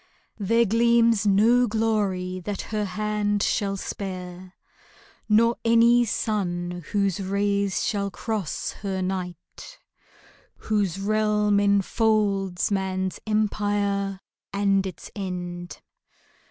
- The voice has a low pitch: No, high, 200 Hz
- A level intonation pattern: Yes, narrow, 2.2 semitones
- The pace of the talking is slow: Yes, slow, 95 wpm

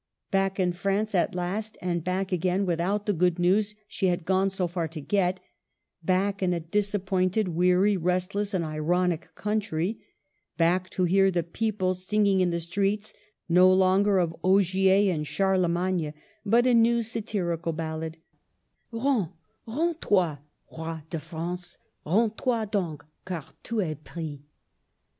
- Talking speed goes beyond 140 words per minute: Yes, average, 150 wpm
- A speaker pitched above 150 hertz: Yes, medium, 185 Hz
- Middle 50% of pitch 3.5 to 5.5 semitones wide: No, average, 2.8 semitones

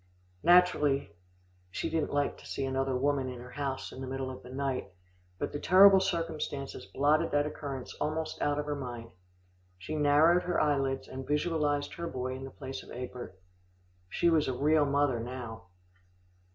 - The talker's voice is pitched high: No, medium, 140 Hz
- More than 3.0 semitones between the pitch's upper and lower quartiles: No, narrow, 2.6 semitones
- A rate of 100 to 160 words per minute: No, average, 175 wpm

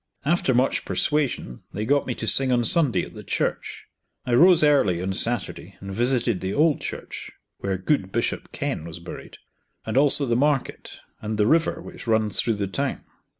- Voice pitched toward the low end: Yes, low, 120 Hz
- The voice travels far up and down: Yes, wide, 5.9 semitones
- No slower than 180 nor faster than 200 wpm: Yes, average, 185 wpm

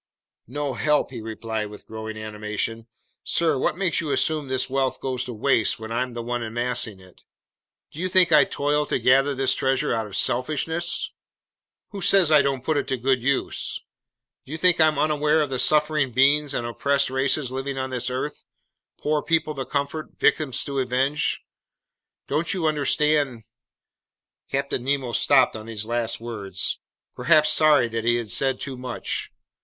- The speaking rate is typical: Yes, average, 175 wpm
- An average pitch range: Yes, average, 3.9 semitones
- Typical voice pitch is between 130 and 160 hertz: Yes, low, 135 Hz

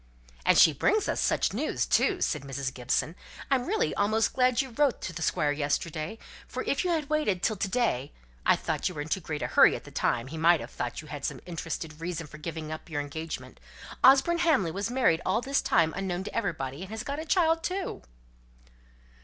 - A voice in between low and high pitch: Yes, medium, 180 Hz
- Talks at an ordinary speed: No, fast, 220 wpm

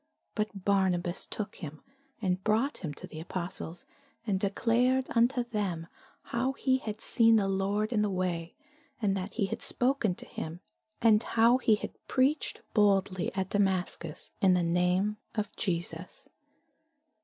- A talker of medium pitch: No, high, 200 Hz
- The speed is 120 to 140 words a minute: No, average, 150 wpm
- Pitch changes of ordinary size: Yes, average, 3.8 semitones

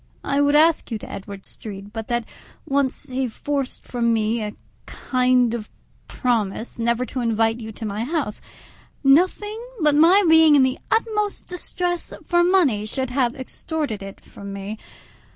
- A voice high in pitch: Yes, very high, 255 Hz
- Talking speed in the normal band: Yes, average, 160 wpm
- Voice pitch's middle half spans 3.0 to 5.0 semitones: No, wide, 5.5 semitones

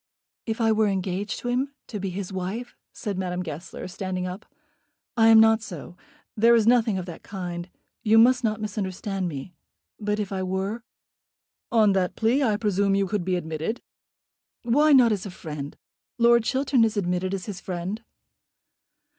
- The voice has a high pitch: Yes, high, 205 Hz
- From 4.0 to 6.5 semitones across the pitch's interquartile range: No, average, 3.6 semitones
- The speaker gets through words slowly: No, average, 175 wpm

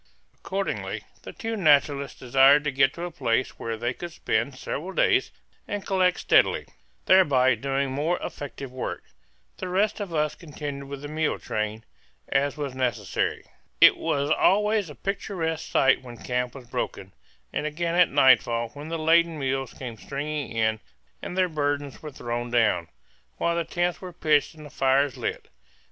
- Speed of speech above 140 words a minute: Yes, average, 165 wpm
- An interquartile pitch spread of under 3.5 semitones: No, average, 4.5 semitones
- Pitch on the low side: No, medium, 145 Hz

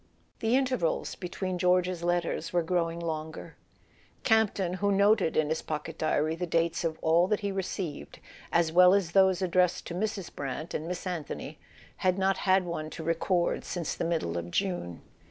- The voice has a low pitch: No, medium, 175 Hz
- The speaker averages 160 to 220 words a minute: Yes, average, 180 wpm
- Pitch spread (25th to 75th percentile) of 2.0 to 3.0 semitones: Yes, average, 2.7 semitones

